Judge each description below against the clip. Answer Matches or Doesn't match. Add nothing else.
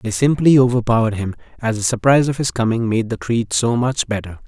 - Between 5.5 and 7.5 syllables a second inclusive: Matches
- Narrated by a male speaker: Matches